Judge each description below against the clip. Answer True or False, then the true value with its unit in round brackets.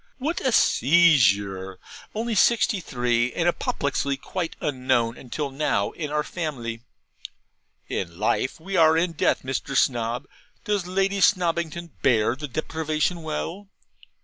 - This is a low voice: False (150 Hz)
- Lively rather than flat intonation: True (6.0 semitones)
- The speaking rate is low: True (125 wpm)